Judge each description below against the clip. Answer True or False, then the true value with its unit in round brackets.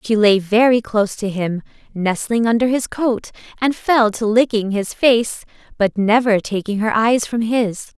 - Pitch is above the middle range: True (220 Hz)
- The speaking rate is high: False (175 wpm)